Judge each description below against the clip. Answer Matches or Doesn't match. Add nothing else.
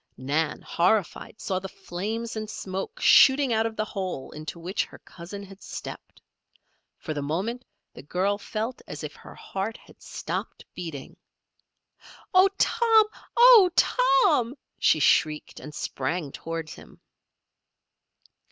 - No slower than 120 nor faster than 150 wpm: Matches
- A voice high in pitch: Matches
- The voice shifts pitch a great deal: Matches